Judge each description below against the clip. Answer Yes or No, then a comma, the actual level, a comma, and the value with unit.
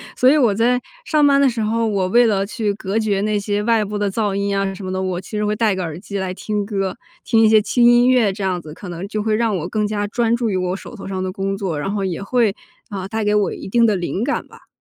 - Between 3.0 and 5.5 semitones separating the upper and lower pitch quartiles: No, narrow, 2.6 semitones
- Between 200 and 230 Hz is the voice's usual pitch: Yes, high, 205 Hz